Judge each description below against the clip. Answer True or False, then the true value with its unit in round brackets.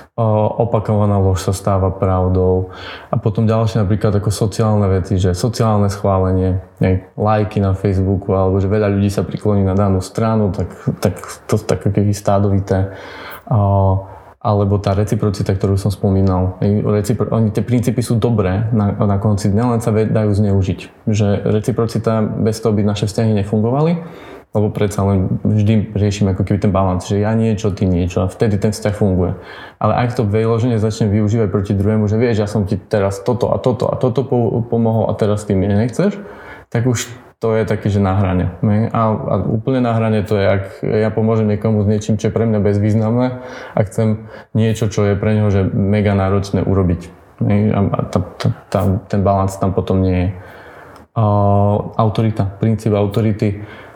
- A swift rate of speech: True (170 wpm)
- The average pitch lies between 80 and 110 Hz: True (105 Hz)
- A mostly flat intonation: True (2.3 semitones)